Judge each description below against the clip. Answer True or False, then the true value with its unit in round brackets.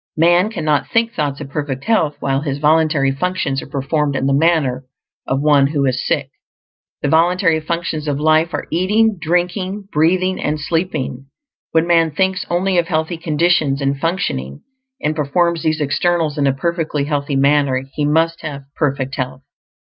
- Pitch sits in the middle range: True (155 Hz)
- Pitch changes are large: False (3.6 semitones)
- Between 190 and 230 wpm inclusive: False (165 wpm)